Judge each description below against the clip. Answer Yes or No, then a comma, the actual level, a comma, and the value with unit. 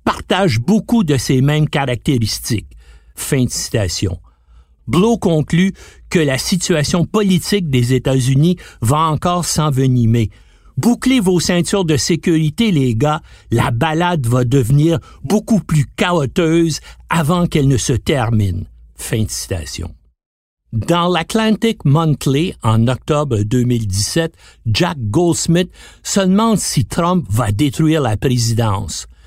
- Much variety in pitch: Yes, wide, 7.3 semitones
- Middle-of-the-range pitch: Yes, medium, 145 Hz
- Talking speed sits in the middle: No, slow, 120 wpm